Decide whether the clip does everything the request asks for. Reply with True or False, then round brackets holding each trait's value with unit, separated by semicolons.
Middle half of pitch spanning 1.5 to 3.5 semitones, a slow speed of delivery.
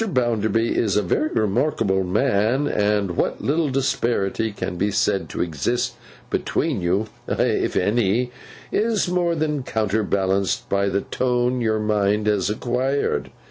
False (4.3 semitones; 125 wpm)